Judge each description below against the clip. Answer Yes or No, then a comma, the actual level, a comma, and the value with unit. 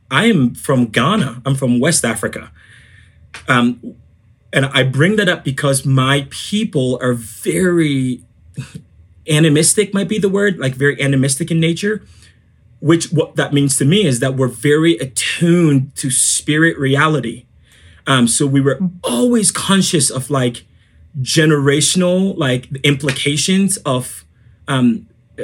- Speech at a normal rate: No, slow, 130 wpm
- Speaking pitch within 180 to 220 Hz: No, medium, 140 Hz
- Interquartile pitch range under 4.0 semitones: No, average, 4.9 semitones